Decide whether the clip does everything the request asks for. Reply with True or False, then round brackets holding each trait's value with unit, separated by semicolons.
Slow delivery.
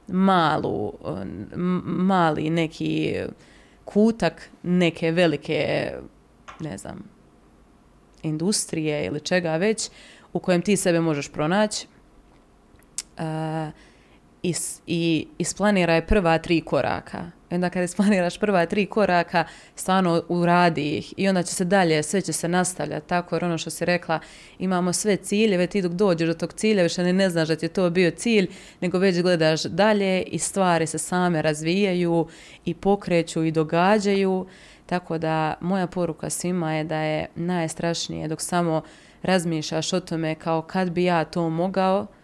False (145 wpm)